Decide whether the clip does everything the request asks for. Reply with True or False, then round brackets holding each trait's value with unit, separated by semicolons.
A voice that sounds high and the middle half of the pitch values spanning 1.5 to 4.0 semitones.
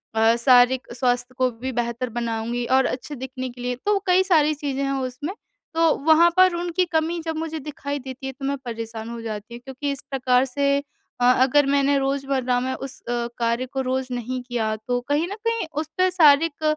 True (265 Hz; 3.5 semitones)